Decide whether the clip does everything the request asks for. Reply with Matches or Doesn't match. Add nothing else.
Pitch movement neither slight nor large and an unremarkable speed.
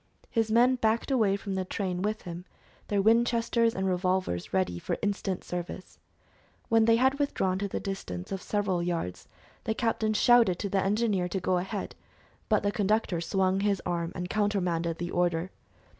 Matches